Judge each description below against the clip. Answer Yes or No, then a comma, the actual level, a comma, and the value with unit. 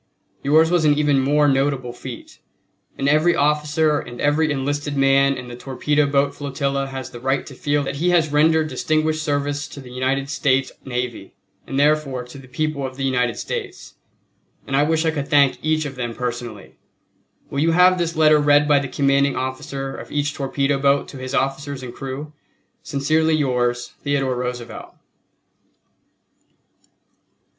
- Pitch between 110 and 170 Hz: Yes, medium, 140 Hz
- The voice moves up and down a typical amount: No, narrow, 2.2 semitones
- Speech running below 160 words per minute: No, average, 165 wpm